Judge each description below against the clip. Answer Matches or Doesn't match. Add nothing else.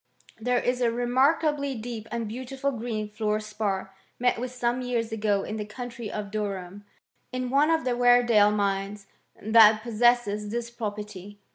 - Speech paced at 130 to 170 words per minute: Matches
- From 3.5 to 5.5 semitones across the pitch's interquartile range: Doesn't match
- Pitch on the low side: Doesn't match